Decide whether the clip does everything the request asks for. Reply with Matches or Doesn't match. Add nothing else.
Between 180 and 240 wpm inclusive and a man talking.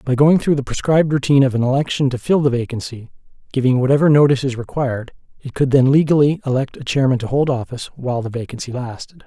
Matches